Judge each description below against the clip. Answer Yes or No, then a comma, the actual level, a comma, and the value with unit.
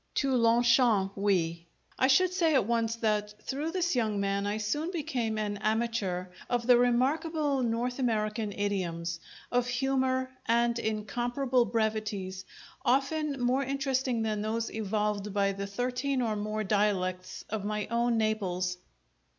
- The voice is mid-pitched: No, high, 225 Hz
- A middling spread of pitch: Yes, average, 3.6 semitones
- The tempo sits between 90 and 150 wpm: Yes, average, 140 wpm